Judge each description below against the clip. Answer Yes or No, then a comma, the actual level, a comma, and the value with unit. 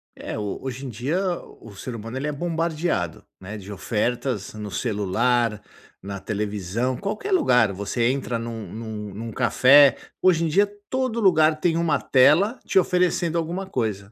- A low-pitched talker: Yes, low, 125 Hz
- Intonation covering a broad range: Yes, wide, 7.8 semitones